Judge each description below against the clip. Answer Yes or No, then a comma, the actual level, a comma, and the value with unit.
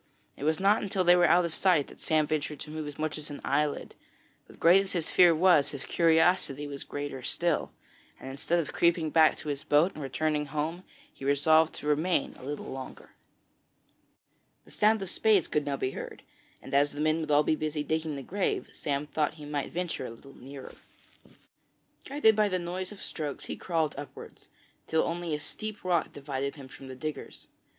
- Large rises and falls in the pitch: No, average, 3.2 semitones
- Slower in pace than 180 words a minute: No, fast, 205 wpm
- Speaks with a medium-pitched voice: Yes, medium, 155 Hz